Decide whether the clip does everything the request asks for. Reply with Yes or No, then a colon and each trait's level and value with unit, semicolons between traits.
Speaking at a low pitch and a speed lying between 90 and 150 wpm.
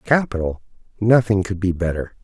Yes: low, 100 Hz; slow, 135 wpm